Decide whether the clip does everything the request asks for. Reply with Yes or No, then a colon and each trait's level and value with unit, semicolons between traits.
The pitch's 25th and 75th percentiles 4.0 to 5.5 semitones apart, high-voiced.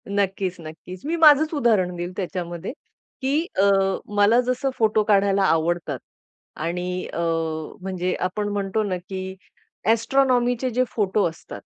Yes: average, 4.8 semitones; high, 200 Hz